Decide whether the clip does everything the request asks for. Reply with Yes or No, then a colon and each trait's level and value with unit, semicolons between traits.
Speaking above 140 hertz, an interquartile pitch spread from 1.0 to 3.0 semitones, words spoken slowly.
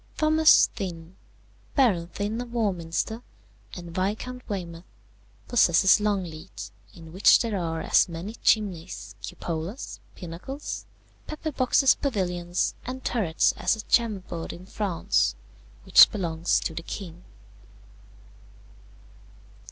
No: high, 190 Hz; average, 5.0 semitones; slow, 105 wpm